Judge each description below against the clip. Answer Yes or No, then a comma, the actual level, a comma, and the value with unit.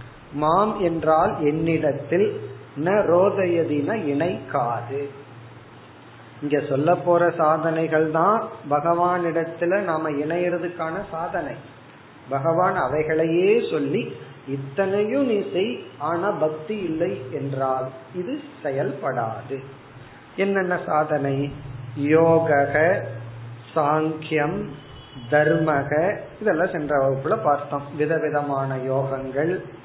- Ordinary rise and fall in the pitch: Yes, average, 3.9 semitones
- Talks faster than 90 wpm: No, average, 80 wpm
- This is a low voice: No, medium, 155 Hz